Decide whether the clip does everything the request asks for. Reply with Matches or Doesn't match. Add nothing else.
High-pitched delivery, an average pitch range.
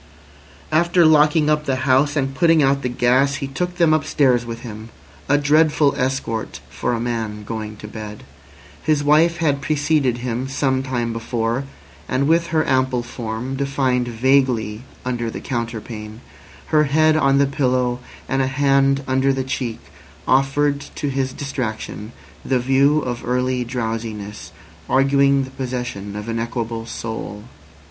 Doesn't match